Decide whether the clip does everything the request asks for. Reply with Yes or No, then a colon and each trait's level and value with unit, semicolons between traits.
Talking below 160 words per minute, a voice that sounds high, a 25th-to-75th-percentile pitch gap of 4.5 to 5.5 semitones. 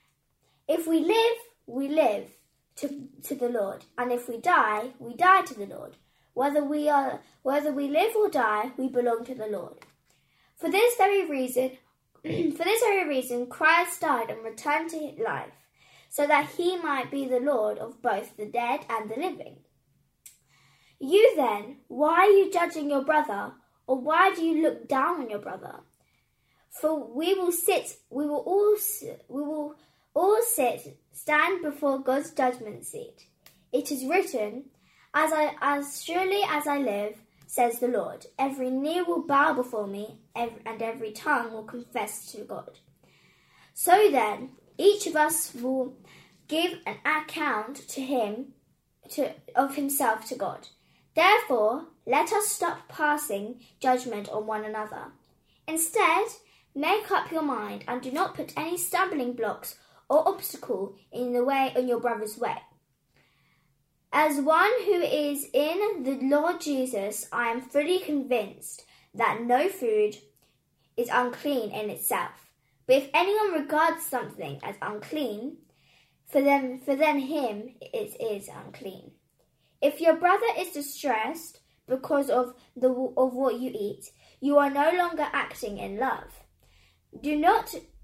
Yes: average, 150 wpm; very high, 285 Hz; average, 5.1 semitones